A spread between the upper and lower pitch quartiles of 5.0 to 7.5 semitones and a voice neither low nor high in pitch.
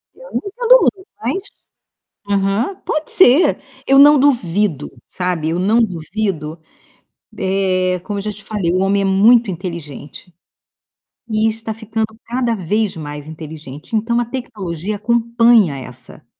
No: average, 5.3 semitones; high, 205 Hz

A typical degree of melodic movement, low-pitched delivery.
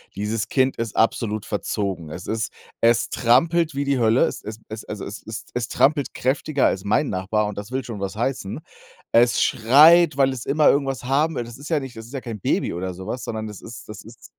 Yes: average, 4.2 semitones; low, 115 Hz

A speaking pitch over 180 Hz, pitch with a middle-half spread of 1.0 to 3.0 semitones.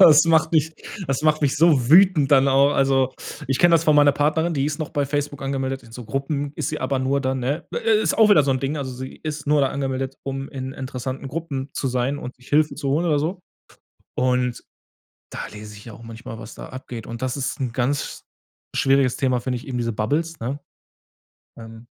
No: low, 135 Hz; narrow, 2.6 semitones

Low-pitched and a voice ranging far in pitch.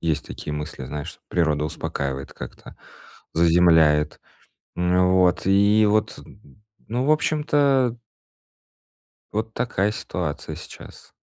Yes: very low, 90 Hz; wide, 6.2 semitones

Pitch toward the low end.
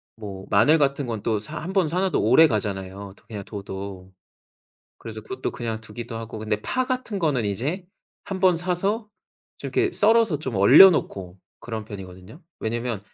Yes: low, 115 Hz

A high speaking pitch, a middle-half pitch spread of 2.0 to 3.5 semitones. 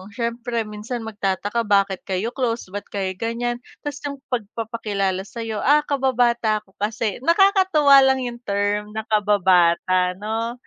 Yes: high, 225 Hz; average, 3.2 semitones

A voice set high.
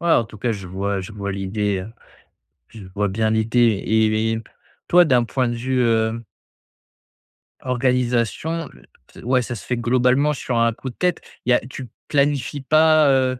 No: low, 120 Hz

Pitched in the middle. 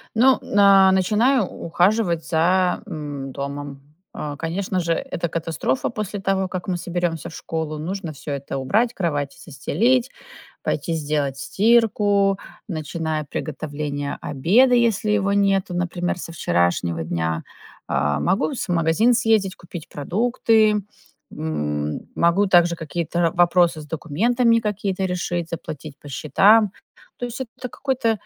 Yes: medium, 175 Hz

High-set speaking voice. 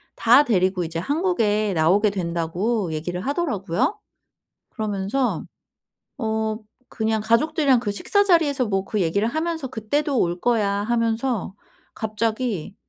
Yes: high, 220 Hz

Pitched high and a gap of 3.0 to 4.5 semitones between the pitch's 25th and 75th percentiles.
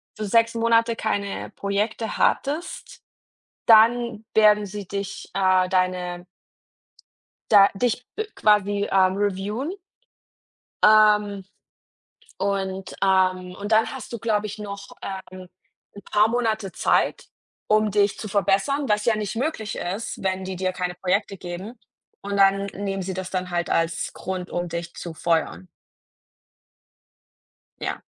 No: high, 200 Hz; narrow, 2.4 semitones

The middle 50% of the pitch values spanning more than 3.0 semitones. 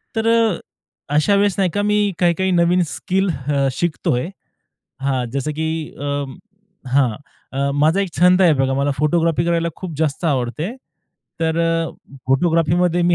Yes: average, 4.4 semitones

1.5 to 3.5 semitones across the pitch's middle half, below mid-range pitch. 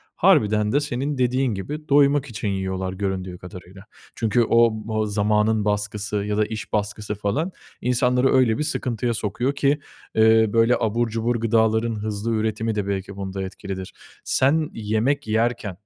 Yes: average, 2.9 semitones; low, 110 Hz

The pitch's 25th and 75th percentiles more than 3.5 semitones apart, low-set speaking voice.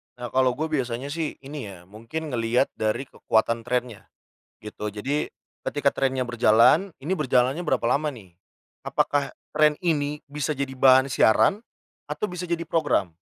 Yes: average, 4.3 semitones; low, 130 Hz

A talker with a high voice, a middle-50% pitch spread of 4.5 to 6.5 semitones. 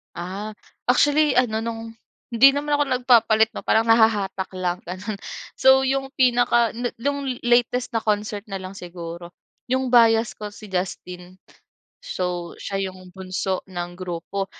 Yes: high, 220 Hz; average, 4.8 semitones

